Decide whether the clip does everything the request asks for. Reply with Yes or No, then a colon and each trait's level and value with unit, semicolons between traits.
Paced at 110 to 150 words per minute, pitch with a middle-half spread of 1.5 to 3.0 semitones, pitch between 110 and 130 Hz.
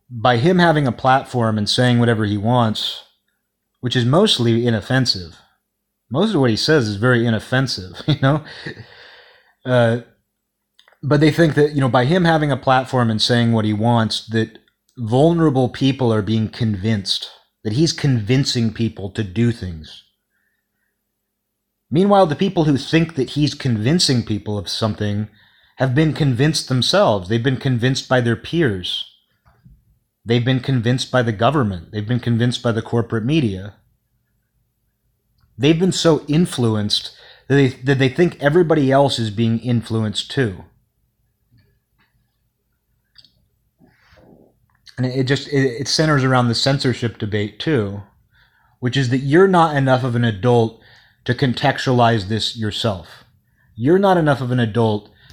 No: average, 145 wpm; average, 3.4 semitones; low, 120 Hz